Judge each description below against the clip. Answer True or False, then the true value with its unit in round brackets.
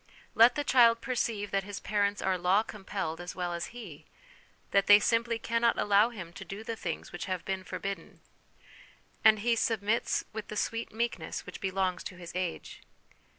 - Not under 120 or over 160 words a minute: False (180 wpm)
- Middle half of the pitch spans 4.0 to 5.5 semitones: False (3.6 semitones)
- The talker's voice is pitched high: True (205 Hz)